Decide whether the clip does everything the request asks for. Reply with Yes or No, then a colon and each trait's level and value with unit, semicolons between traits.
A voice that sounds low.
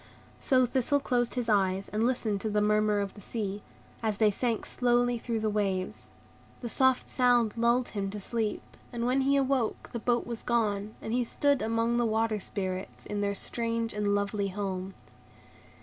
No: high, 225 Hz